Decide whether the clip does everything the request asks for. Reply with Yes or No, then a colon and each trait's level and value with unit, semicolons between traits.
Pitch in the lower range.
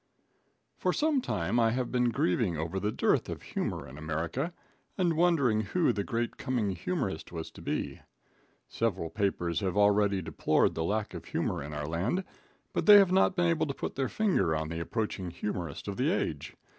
Yes: low, 105 Hz